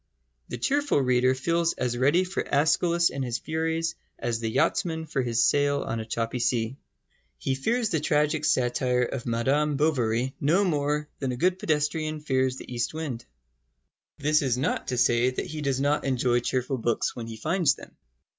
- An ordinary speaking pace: Yes, average, 180 wpm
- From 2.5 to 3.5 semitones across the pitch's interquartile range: No, average, 4.0 semitones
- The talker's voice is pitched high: No, low, 135 Hz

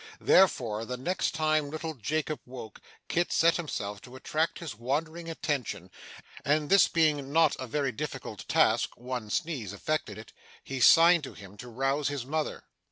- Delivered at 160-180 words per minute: Yes, average, 165 wpm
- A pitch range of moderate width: Yes, average, 4.4 semitones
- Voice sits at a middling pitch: Yes, medium, 145 Hz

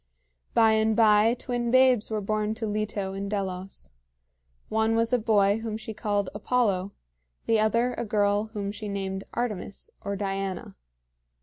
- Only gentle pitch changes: Yes, narrow, 2.0 semitones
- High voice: Yes, high, 215 Hz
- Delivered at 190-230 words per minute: No, average, 150 wpm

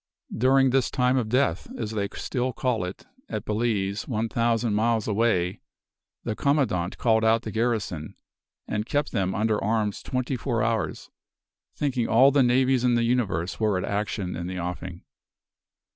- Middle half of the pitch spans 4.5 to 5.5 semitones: No, average, 3.6 semitones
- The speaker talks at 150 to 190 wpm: Yes, average, 160 wpm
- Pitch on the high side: No, low, 115 Hz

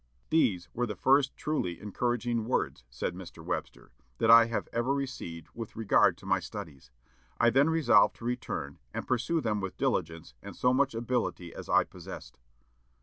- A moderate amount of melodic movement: No, wide, 5.9 semitones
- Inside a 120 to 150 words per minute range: No, average, 165 wpm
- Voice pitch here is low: Yes, low, 115 Hz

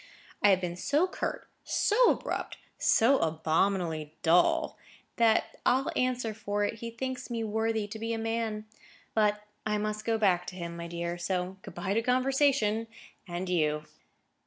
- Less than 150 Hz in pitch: No, high, 210 Hz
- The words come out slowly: No, average, 160 wpm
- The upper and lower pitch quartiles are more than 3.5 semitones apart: Yes, average, 4.5 semitones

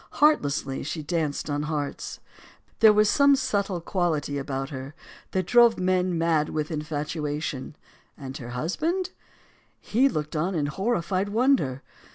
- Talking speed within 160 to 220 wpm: No, slow, 135 wpm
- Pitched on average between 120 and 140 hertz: No, medium, 160 Hz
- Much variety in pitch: Yes, wide, 5.8 semitones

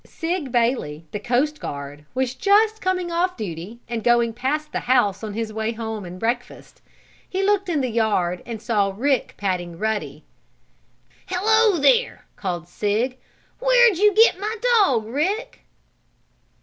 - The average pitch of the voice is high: Yes, high, 245 Hz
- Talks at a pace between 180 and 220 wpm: No, average, 150 wpm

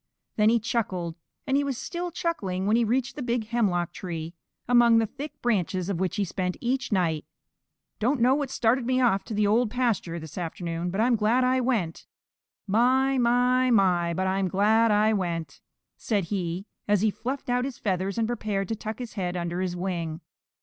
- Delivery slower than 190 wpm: No, average, 195 wpm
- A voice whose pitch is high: Yes, high, 215 Hz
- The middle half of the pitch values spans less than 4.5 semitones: No, average, 5.1 semitones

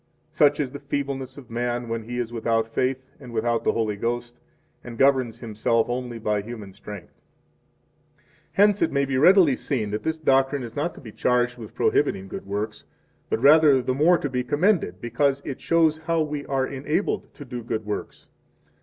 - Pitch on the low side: Yes, low, 125 Hz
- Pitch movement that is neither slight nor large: Yes, average, 3.9 semitones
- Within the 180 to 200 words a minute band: Yes, average, 190 wpm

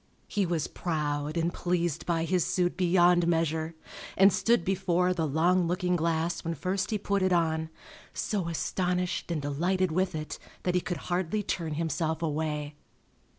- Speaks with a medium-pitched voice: Yes, medium, 175 Hz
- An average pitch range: No, narrow, 2.3 semitones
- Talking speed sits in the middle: Yes, average, 160 wpm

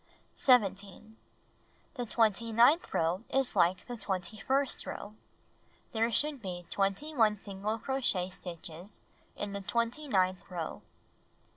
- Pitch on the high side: Yes, high, 210 Hz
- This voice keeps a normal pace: No, slow, 120 wpm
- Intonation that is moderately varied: Yes, average, 4.2 semitones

